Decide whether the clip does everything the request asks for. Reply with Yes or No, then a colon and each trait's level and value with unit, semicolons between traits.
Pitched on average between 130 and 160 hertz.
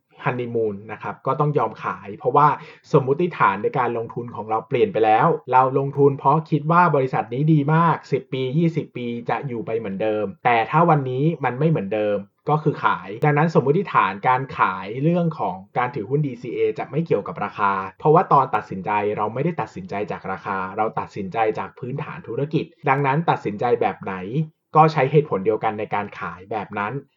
Yes: medium, 140 Hz